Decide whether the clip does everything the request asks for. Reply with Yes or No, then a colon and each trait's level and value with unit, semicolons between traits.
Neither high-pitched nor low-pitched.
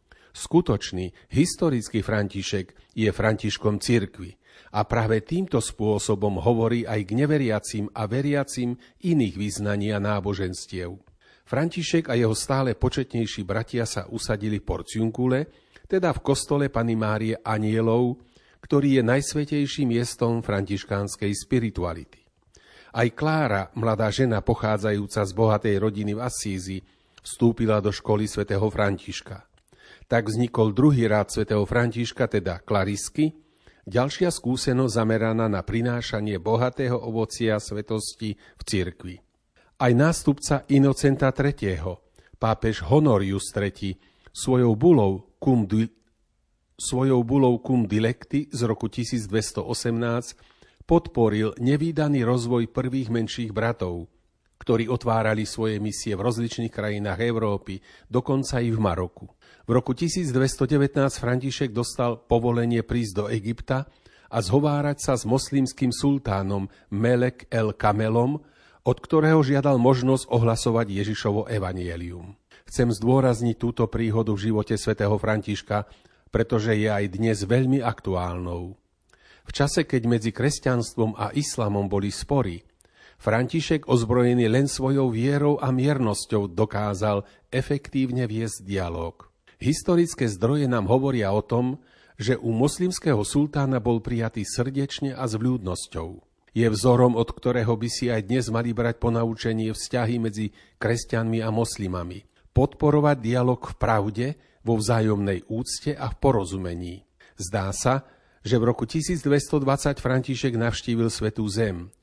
No: low, 115 Hz